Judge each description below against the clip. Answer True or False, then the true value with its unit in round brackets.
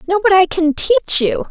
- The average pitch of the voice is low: False (365 Hz)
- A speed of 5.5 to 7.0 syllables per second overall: True (5.7 syllables/s)